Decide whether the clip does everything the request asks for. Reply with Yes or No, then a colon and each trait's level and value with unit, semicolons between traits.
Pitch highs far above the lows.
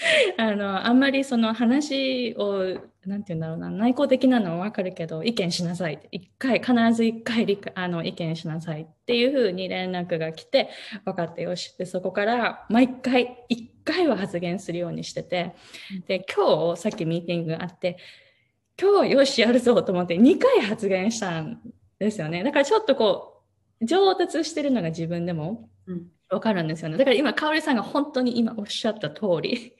Yes: wide, 6.0 semitones